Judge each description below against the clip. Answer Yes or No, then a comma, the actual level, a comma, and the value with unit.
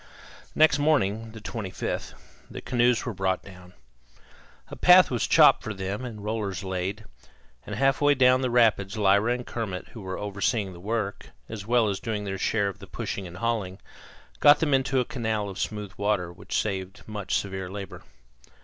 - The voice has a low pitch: Yes, low, 105 Hz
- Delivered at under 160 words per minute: No, average, 180 wpm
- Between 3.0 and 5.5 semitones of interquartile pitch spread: Yes, average, 3.7 semitones